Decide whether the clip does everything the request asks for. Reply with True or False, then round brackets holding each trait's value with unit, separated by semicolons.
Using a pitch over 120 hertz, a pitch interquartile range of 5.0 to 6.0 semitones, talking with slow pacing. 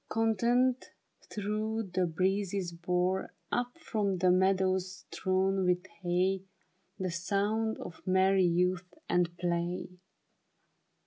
False (190 Hz; 2.4 semitones; 105 wpm)